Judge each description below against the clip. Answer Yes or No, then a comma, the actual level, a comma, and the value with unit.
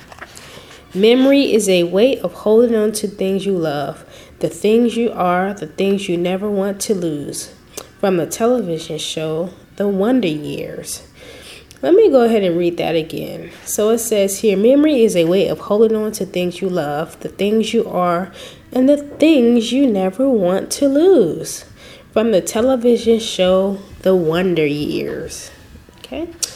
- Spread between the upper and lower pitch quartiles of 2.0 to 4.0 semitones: No, average, 4.8 semitones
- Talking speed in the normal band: Yes, average, 165 wpm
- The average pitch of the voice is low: No, high, 200 Hz